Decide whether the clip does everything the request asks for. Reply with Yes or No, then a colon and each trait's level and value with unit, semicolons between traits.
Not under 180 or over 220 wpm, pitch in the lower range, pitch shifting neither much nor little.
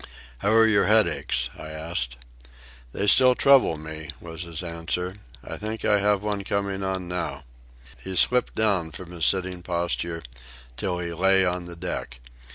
No: average, 165 wpm; very low, 90 Hz; average, 3.3 semitones